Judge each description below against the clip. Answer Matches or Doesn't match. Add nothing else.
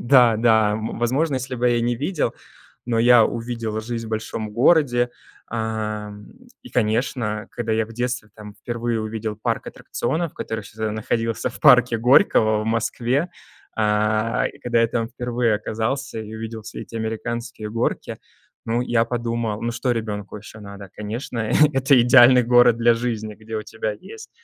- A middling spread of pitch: Doesn't match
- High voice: Doesn't match